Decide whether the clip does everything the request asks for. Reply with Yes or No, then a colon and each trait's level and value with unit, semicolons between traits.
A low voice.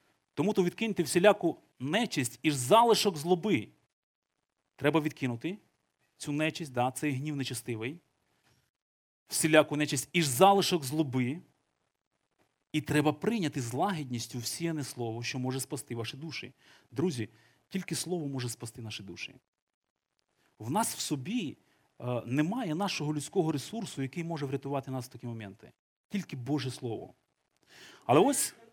No: medium, 145 Hz